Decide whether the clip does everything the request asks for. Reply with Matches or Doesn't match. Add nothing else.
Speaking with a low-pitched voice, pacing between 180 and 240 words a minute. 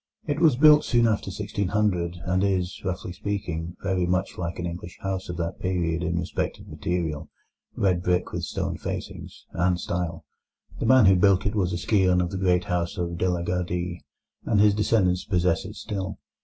Matches